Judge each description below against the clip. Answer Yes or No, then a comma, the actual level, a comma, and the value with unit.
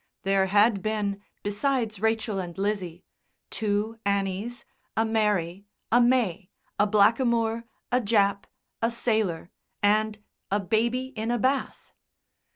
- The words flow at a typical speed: No, slow, 120 wpm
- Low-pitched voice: No, high, 215 Hz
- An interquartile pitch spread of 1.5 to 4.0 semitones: Yes, narrow, 2.4 semitones